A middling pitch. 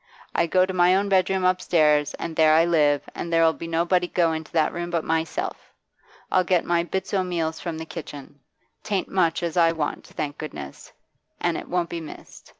Yes: medium, 170 Hz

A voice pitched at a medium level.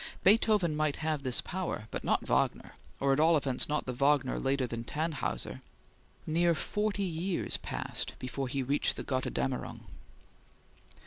Yes: medium, 150 Hz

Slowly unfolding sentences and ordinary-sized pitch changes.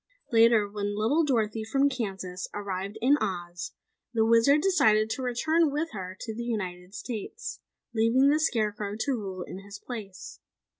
No: average, 155 wpm; average, 4.2 semitones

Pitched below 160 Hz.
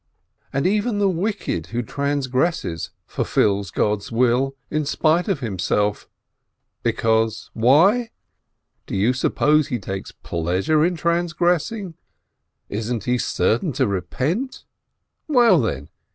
Yes: low, 135 Hz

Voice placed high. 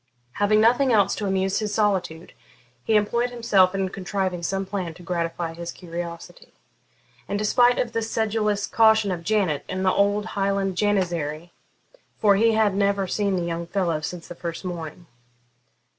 Yes: high, 195 Hz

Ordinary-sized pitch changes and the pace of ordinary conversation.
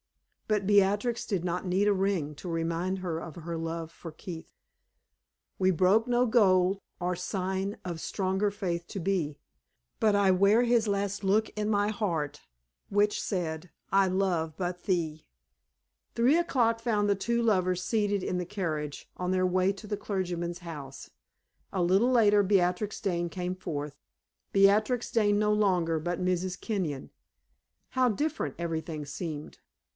Yes: average, 3.2 semitones; average, 150 wpm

